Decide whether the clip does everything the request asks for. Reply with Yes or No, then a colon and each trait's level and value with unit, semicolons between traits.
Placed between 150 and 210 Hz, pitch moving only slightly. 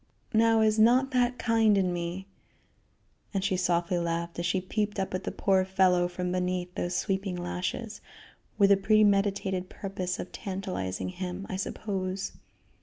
Yes: high, 190 Hz; narrow, 2.3 semitones